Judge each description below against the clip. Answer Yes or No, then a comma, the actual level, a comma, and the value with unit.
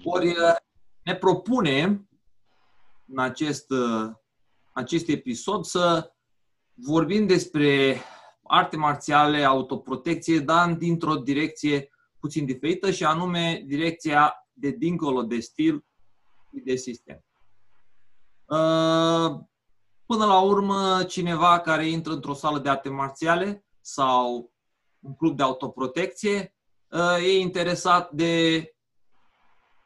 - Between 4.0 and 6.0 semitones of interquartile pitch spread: Yes, average, 4.6 semitones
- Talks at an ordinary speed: No, slow, 95 wpm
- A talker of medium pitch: Yes, medium, 160 Hz